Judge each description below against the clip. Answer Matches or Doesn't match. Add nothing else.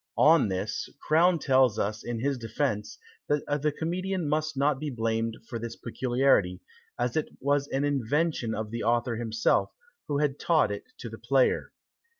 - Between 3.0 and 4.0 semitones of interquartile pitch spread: Doesn't match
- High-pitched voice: Doesn't match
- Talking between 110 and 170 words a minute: Matches